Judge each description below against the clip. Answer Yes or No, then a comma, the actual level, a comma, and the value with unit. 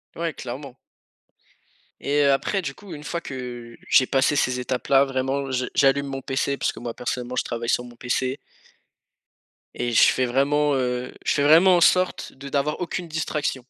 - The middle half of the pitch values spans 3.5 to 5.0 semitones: No, average, 2.7 semitones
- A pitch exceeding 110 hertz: Yes, low, 135 Hz